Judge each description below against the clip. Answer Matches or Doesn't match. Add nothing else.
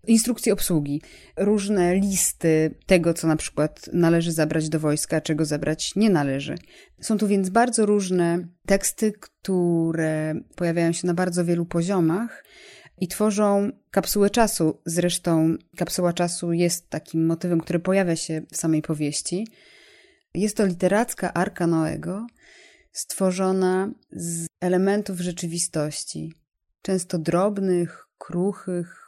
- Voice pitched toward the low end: Doesn't match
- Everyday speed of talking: Matches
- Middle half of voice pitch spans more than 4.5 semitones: Doesn't match